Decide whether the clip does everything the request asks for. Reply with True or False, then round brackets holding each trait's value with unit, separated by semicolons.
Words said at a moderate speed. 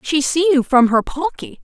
False (220 wpm)